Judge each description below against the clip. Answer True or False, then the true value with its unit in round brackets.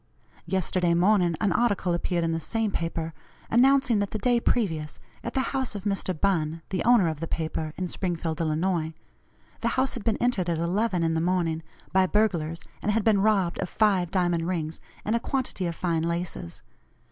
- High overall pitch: False (180 Hz)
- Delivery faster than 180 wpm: True (190 wpm)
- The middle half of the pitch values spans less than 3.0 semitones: False (4.3 semitones)